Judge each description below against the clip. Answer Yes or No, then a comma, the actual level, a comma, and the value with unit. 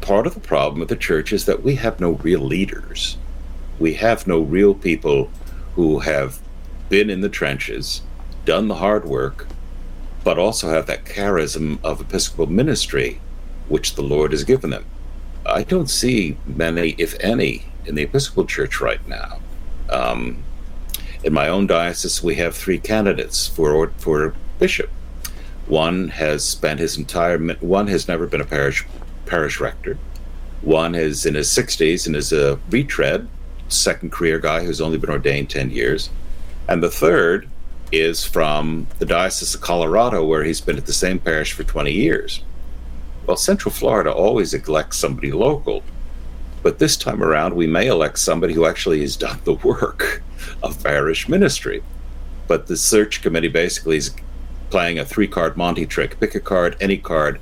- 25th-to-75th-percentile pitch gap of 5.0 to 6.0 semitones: Yes, wide, 5.5 semitones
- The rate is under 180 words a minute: Yes, average, 165 wpm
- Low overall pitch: Yes, very low, 65 Hz